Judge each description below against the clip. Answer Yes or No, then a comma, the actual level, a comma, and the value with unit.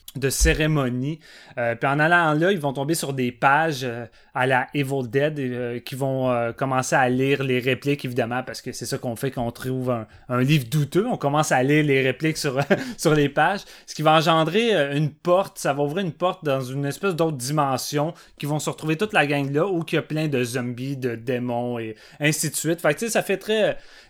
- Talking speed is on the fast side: Yes, fast, 235 wpm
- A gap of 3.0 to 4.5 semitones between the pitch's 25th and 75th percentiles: Yes, average, 3.7 semitones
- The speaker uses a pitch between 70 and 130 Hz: No, medium, 140 Hz